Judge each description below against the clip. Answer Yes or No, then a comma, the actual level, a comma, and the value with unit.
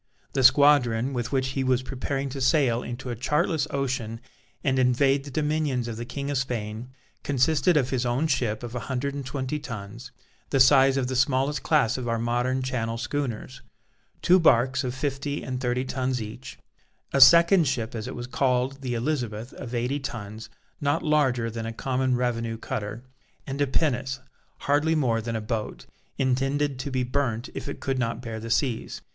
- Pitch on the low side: Yes, low, 130 Hz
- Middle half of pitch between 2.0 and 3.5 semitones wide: Yes, average, 2.7 semitones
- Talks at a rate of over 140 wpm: Yes, average, 185 wpm